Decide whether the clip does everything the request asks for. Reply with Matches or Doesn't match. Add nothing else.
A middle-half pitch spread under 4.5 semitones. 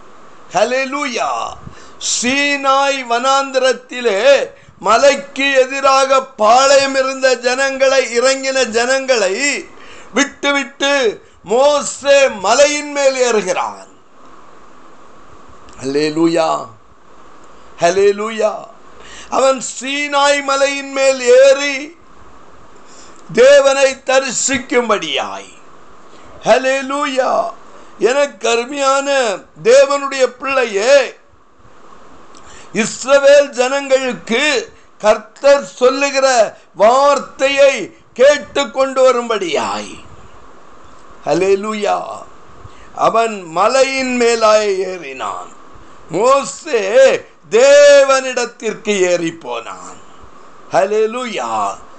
Matches